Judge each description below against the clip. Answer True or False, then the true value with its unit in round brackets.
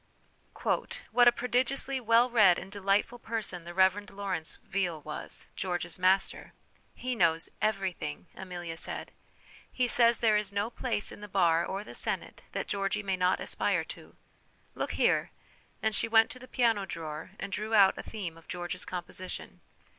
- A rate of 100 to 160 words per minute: False (175 wpm)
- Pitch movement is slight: False (4.0 semitones)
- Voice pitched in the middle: False (195 Hz)